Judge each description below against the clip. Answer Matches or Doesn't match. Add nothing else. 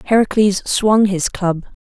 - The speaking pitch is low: Doesn't match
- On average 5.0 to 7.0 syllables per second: Doesn't match